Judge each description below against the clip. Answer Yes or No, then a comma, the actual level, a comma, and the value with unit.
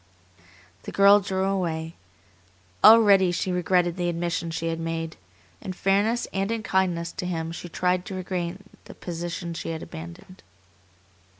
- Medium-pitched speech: Yes, medium, 180 Hz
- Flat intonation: Yes, narrow, 2.2 semitones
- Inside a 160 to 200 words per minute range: No, average, 145 wpm